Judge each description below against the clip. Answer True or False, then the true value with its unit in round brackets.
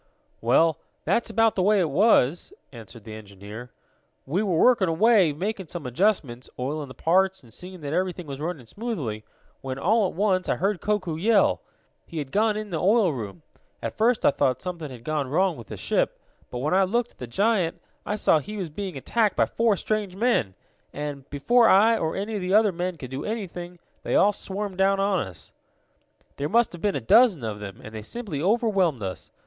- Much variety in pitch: True (7.1 semitones)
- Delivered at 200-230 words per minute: True (205 wpm)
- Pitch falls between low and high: True (180 Hz)